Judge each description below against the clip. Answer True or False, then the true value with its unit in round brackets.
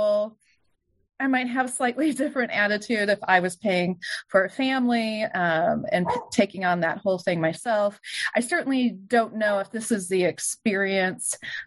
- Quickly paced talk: False (165 wpm)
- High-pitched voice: True (215 Hz)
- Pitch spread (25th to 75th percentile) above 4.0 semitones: True (4.5 semitones)